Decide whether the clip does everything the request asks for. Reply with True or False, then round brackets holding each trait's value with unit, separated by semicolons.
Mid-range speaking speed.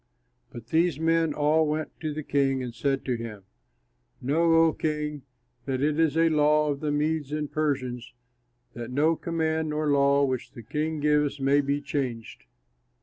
True (170 wpm)